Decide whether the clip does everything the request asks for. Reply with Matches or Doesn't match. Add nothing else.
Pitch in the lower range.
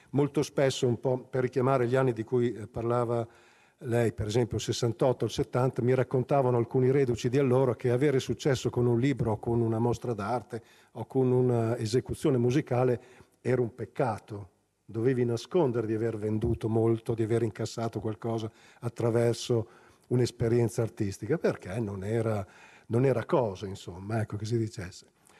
Matches